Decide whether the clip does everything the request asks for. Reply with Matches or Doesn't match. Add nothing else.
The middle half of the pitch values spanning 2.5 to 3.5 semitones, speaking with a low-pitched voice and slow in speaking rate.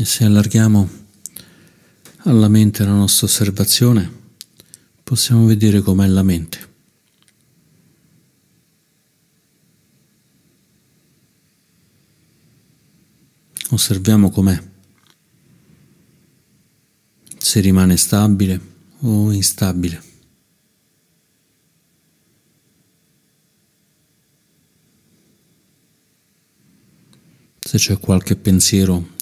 Matches